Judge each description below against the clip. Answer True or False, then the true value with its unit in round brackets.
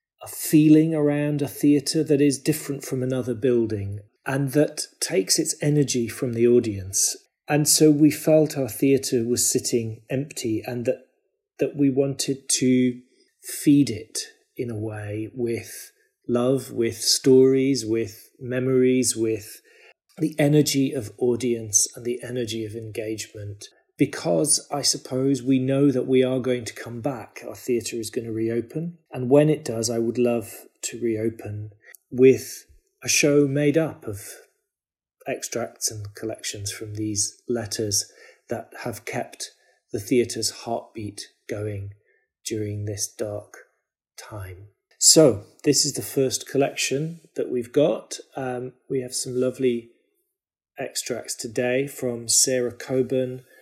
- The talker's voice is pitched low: True (125 Hz)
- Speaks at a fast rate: False (140 wpm)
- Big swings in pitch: False (4.1 semitones)